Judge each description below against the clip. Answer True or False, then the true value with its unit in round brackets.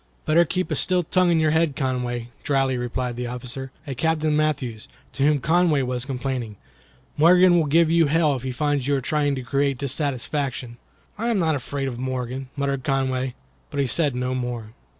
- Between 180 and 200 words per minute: True (190 wpm)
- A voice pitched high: False (140 Hz)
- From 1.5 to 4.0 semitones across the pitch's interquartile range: True (3.4 semitones)